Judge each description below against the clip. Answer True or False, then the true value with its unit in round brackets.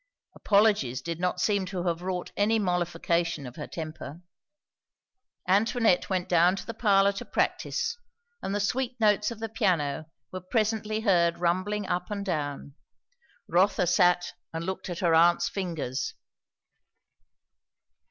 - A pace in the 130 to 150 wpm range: True (140 wpm)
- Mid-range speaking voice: True (180 Hz)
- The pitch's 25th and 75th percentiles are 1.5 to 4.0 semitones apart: True (3.4 semitones)